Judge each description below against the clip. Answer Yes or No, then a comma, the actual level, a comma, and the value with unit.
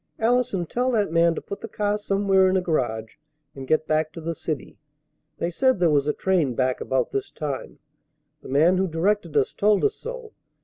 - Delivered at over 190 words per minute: Yes, fast, 205 wpm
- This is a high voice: No, medium, 175 Hz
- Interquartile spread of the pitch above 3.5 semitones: Yes, wide, 5.4 semitones